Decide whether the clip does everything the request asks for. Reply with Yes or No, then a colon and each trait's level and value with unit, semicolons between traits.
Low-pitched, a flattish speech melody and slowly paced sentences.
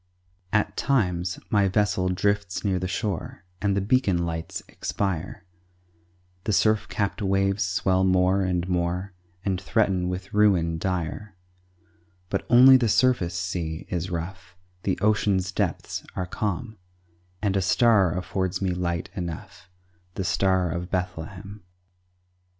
Yes: very low, 95 Hz; narrow, 2.2 semitones; slow, 130 wpm